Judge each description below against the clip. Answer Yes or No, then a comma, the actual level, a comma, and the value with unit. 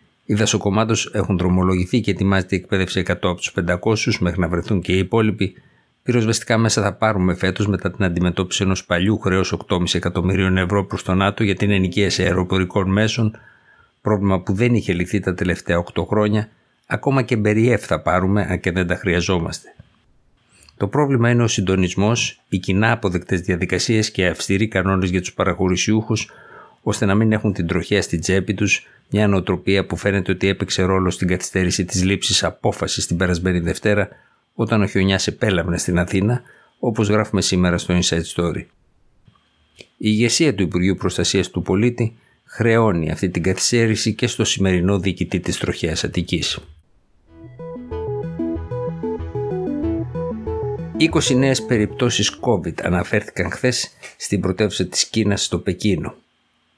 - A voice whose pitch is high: No, low, 100 Hz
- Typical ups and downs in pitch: Yes, average, 3.1 semitones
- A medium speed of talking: Yes, average, 145 wpm